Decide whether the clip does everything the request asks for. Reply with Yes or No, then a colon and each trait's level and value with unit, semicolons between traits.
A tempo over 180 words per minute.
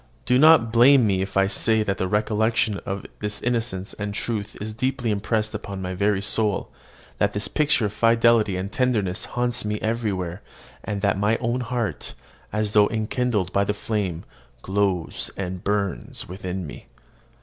No: average, 165 wpm